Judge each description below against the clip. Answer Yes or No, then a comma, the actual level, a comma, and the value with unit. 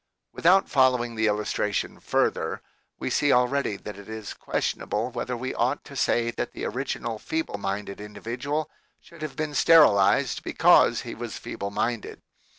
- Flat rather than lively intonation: No, average, 5.0 semitones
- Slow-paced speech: No, average, 155 wpm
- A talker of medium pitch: No, low, 120 Hz